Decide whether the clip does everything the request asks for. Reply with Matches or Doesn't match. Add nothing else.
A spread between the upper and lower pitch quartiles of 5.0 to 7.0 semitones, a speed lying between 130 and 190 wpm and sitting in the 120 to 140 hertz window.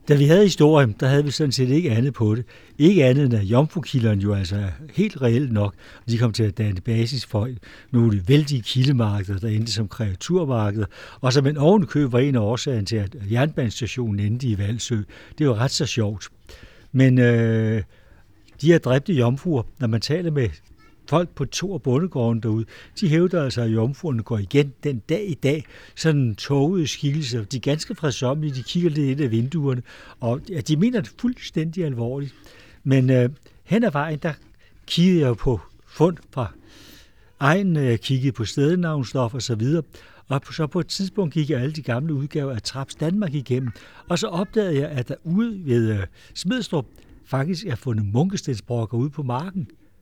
Matches